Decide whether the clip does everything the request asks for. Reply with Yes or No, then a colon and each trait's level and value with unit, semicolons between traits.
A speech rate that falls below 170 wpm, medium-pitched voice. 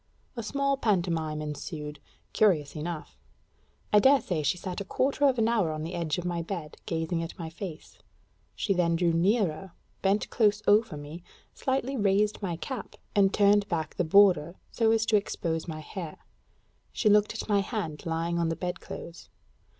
No: average, 180 wpm; medium, 180 Hz